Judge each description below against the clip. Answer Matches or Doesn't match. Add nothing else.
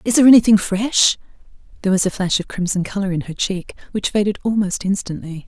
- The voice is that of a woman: Matches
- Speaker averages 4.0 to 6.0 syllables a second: Doesn't match